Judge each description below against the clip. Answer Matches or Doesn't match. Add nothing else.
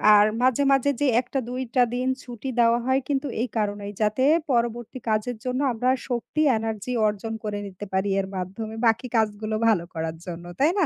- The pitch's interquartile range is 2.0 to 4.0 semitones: Matches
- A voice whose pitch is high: Matches